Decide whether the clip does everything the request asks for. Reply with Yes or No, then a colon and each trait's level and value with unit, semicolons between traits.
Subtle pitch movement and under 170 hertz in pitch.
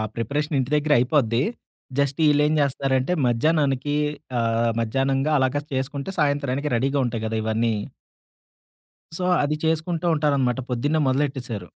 No: average, 3.3 semitones; low, 135 Hz